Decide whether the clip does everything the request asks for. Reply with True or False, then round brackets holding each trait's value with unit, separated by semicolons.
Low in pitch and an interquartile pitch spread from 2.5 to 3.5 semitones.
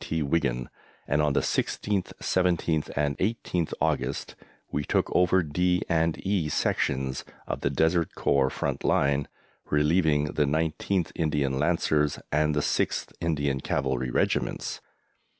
True (75 Hz; 3.0 semitones)